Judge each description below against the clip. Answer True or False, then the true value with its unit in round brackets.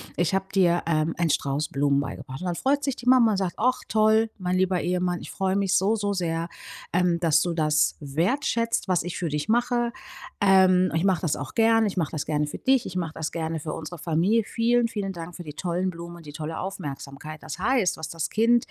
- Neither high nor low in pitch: True (180 Hz)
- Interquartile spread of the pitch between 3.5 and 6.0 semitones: True (4.4 semitones)